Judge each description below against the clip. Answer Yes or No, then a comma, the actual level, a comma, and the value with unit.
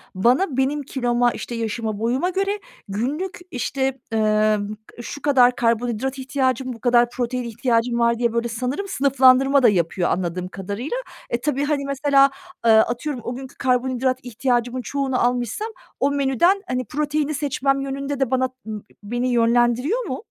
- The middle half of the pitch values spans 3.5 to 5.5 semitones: No, average, 2.8 semitones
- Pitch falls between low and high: No, very high, 255 Hz